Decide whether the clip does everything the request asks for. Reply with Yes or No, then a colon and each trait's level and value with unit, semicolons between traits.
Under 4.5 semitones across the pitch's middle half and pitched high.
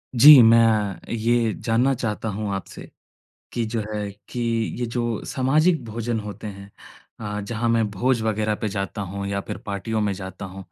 No: average, 2.7 semitones; low, 110 Hz